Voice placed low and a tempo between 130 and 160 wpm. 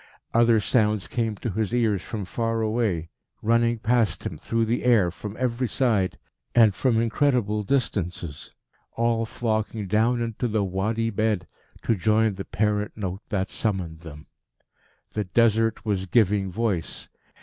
Yes: low, 110 Hz; average, 145 wpm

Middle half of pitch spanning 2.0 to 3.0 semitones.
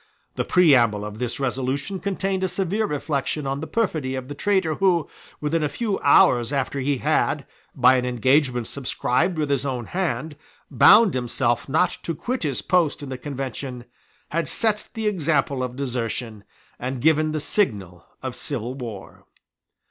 No: average, 4.8 semitones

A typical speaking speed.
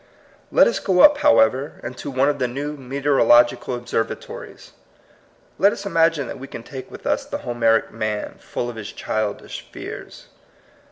Yes: average, 165 wpm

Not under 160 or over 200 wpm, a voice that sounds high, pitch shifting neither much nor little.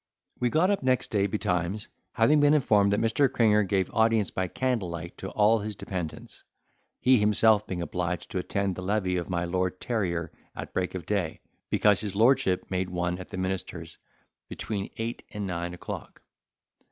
No: average, 175 wpm; low, 100 Hz; average, 3.6 semitones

